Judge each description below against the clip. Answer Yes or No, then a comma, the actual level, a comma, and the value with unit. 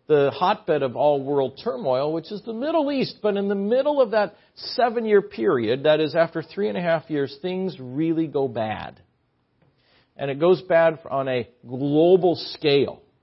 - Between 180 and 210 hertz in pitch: No, medium, 165 Hz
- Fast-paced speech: No, average, 180 wpm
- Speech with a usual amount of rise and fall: No, wide, 6.3 semitones